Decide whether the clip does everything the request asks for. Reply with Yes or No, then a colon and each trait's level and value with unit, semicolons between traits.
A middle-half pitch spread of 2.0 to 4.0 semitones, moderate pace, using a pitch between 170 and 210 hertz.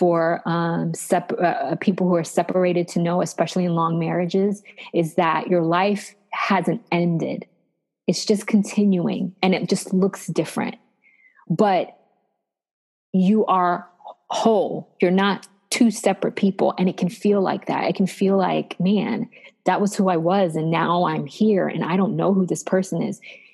Yes: narrow, 2.6 semitones; average, 165 wpm; medium, 185 Hz